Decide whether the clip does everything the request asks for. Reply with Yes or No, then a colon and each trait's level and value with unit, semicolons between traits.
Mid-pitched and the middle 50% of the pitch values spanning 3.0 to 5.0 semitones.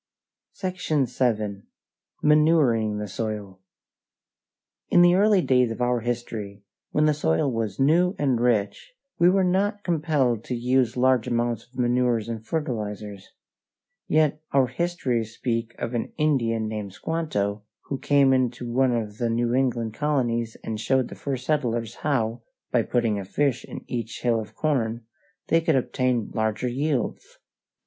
No: low, 125 Hz; average, 4.4 semitones